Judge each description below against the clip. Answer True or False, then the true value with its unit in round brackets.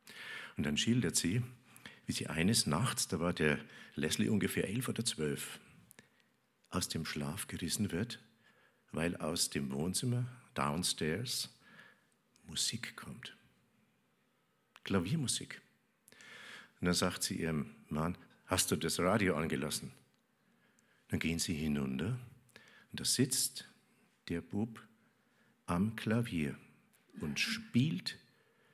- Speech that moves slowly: True (110 wpm)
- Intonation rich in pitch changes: True (6.5 semitones)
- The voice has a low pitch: True (95 Hz)